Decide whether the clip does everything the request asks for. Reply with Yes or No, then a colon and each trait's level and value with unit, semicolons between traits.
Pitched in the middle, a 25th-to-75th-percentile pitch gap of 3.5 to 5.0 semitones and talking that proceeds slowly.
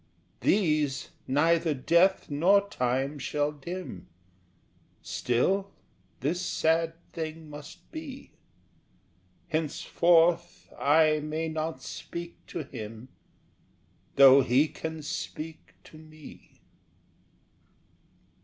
No: medium, 155 Hz; average, 2.8 semitones; slow, 85 wpm